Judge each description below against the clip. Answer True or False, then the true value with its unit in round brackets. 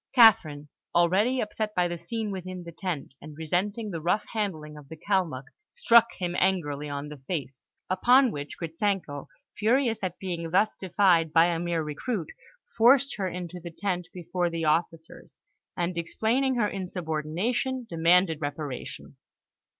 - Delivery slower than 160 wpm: True (150 wpm)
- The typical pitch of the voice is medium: True (175 Hz)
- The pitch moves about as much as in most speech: True (4.4 semitones)